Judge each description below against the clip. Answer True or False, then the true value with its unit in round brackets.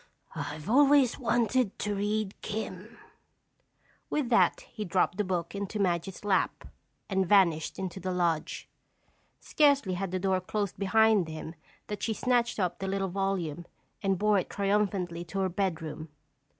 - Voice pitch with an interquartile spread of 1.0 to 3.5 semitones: True (2.8 semitones)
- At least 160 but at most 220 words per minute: False (150 wpm)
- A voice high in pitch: True (195 Hz)